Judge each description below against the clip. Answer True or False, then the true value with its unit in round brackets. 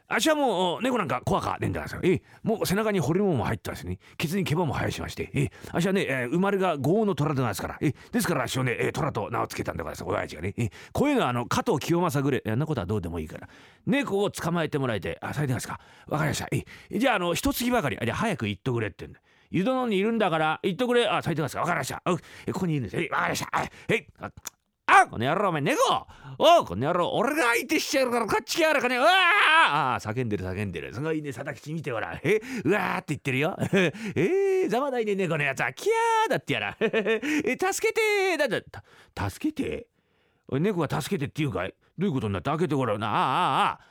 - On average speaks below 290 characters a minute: False (495 characters per minute)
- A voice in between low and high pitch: True (170 Hz)